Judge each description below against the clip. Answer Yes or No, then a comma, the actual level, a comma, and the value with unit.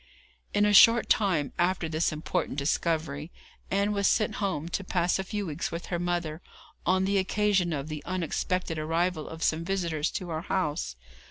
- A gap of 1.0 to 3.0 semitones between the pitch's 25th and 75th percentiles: No, average, 3.4 semitones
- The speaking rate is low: No, average, 175 wpm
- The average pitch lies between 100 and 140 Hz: No, medium, 175 Hz